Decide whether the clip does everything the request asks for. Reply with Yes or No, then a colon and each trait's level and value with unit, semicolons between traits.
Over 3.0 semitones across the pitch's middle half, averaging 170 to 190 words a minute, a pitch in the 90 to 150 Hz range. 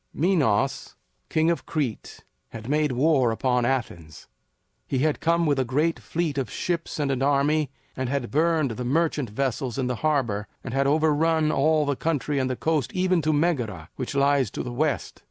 Yes: average, 3.7 semitones; average, 185 wpm; medium, 140 Hz